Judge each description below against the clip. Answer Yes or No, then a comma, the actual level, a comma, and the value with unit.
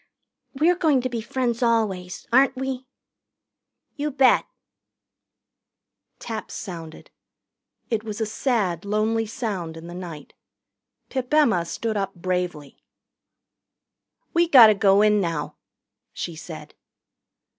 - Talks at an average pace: No, slow, 115 wpm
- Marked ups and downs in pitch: Yes, wide, 6.0 semitones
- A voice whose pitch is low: No, high, 215 Hz